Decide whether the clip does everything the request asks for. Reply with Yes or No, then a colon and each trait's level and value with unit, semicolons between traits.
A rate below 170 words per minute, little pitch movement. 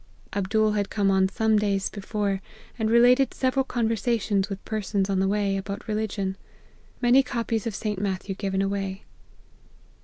Yes: average, 155 wpm; narrow, 2.3 semitones